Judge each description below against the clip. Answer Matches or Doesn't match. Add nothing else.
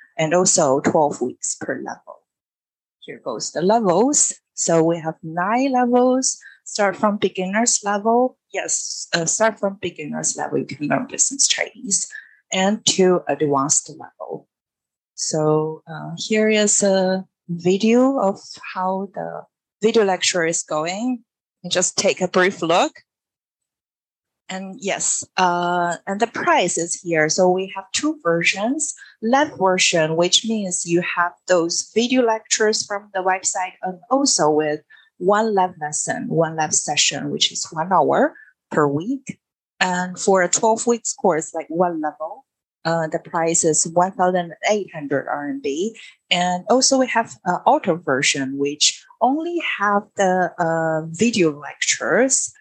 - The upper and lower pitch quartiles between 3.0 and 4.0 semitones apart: Doesn't match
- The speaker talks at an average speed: Matches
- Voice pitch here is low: Doesn't match